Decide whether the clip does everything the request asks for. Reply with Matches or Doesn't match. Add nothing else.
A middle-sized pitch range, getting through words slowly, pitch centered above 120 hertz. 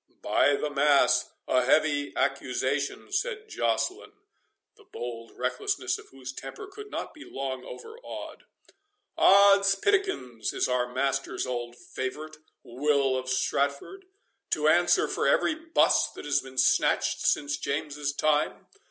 Doesn't match